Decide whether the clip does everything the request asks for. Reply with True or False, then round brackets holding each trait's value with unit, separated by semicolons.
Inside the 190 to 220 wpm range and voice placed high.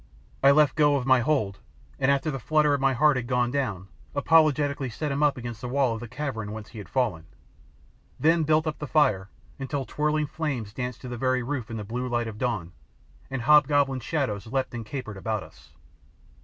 False (205 wpm; 130 Hz)